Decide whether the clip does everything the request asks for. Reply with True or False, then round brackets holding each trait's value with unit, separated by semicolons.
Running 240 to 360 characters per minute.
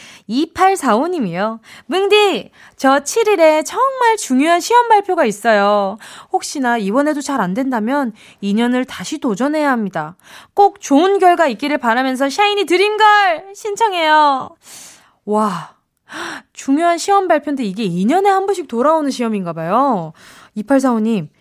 True (265 characters per minute)